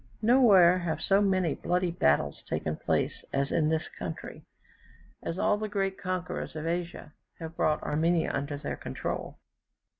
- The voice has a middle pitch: Yes, medium, 175 Hz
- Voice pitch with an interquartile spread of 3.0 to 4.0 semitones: Yes, average, 3.3 semitones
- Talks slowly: No, average, 150 wpm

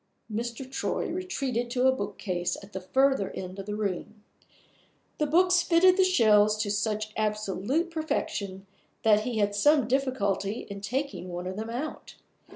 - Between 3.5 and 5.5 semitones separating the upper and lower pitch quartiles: Yes, average, 5.2 semitones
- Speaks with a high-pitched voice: Yes, high, 220 Hz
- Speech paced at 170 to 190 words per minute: No, average, 160 wpm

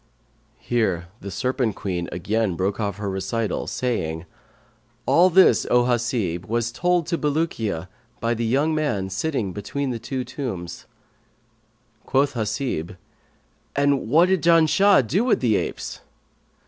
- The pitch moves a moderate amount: No, wide, 6.5 semitones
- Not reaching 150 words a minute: Yes, slow, 135 wpm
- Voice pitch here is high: No, low, 120 Hz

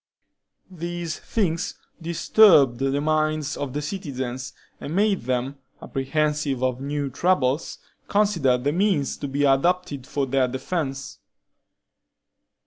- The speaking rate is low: Yes, slow, 115 wpm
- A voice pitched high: No, medium, 145 Hz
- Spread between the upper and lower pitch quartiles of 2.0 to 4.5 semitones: Yes, average, 4.1 semitones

